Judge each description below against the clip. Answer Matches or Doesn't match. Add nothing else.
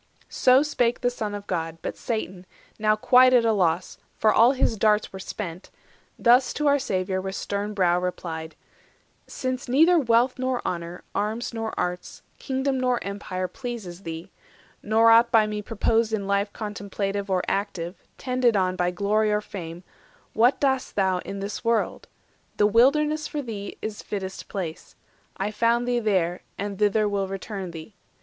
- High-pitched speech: Matches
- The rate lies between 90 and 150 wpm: Doesn't match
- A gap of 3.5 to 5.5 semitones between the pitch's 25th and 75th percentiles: Matches